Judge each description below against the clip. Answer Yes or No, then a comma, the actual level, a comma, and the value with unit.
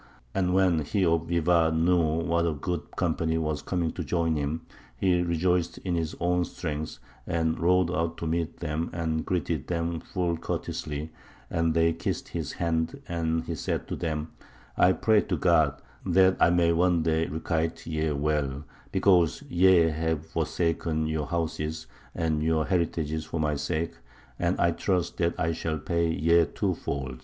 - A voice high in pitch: No, very low, 80 Hz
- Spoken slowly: No, average, 165 wpm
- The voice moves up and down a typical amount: No, narrow, 1.6 semitones